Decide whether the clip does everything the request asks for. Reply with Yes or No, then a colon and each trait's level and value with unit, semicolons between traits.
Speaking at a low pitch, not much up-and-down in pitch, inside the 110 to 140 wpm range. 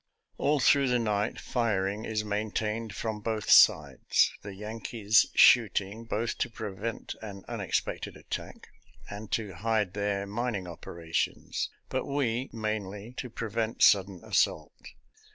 Yes: low, 110 Hz; narrow, 2.2 semitones; slow, 135 wpm